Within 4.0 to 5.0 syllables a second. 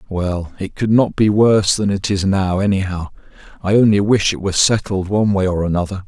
No: 5.5 syllables/s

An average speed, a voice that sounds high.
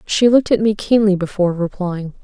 Yes: average, 190 wpm; high, 195 Hz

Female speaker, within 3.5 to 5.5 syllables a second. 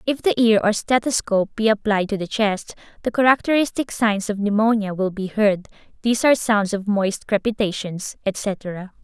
Yes: female; 5.0 syllables/s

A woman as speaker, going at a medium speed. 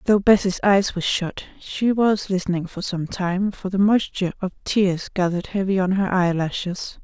Yes: female; average, 180 wpm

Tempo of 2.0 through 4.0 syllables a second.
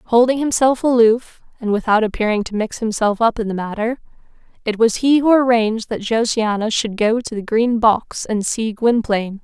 No: 5.0 syllables/s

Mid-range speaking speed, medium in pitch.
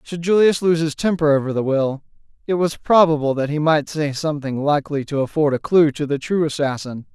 No: fast, 210 wpm; medium, 150 Hz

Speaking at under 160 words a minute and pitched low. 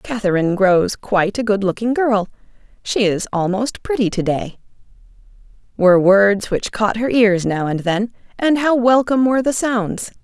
No: average, 150 wpm; high, 215 Hz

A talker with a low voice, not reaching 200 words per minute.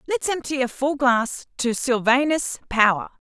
No: very high, 260 Hz; average, 145 wpm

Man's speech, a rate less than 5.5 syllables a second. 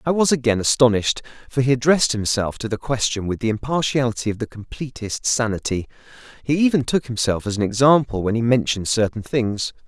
No: male; 6.0 syllables/s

